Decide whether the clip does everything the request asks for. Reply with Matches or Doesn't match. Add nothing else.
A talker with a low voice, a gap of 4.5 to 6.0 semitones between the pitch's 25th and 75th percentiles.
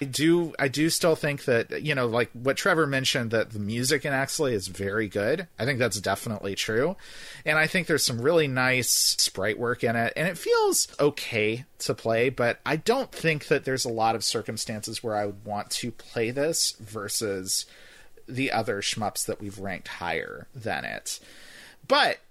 Matches